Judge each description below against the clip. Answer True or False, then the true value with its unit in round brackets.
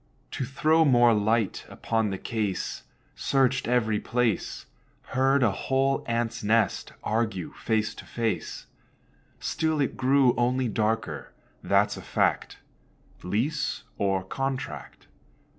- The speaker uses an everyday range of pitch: True (3.7 semitones)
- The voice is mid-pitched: False (115 Hz)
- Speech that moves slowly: True (115 wpm)